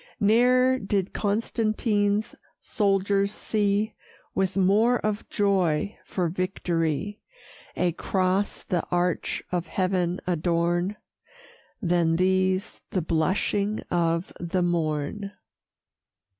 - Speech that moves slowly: Yes, slow, 90 wpm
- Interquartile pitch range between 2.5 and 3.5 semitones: Yes, average, 2.9 semitones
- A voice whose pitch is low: No, high, 190 Hz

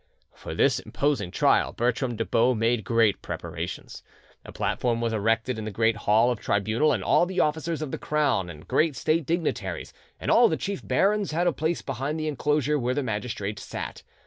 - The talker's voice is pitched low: Yes, low, 125 Hz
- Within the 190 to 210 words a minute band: Yes, average, 195 wpm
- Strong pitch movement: Yes, wide, 5.8 semitones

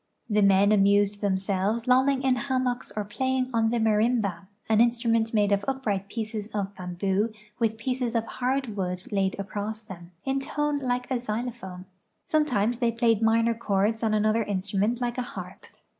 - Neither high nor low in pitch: No, high, 225 Hz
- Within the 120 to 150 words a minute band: No, average, 165 wpm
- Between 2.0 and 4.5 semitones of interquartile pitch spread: Yes, average, 3.3 semitones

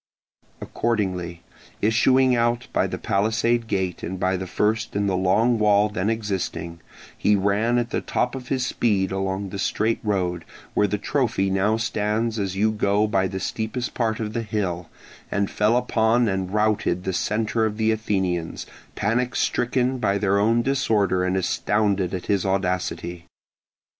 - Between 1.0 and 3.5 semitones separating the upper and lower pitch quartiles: Yes, average, 3.0 semitones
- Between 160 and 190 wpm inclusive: Yes, average, 165 wpm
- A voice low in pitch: Yes, low, 105 Hz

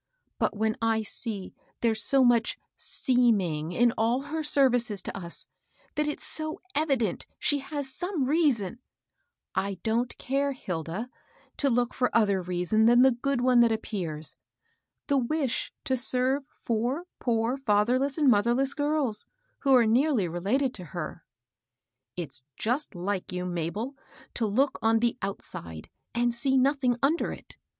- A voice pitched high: Yes, high, 240 Hz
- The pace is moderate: Yes, average, 160 wpm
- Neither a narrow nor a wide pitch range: Yes, average, 5.0 semitones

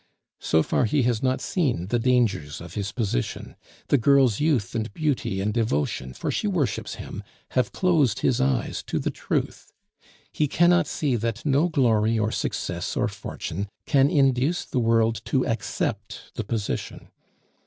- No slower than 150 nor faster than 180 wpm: Yes, average, 160 wpm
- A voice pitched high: No, low, 120 Hz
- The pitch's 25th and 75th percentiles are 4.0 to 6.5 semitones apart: Yes, average, 4.5 semitones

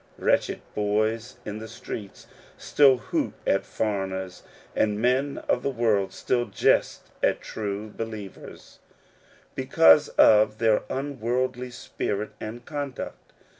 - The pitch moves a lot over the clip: No, average, 3.1 semitones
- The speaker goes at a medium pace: No, slow, 115 wpm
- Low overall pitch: Yes, low, 110 Hz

